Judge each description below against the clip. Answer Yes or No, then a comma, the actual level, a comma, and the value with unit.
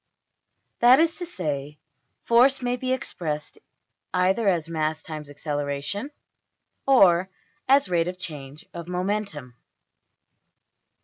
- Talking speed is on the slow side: Yes, slow, 110 wpm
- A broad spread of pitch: Yes, wide, 7.7 semitones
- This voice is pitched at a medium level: Yes, medium, 180 Hz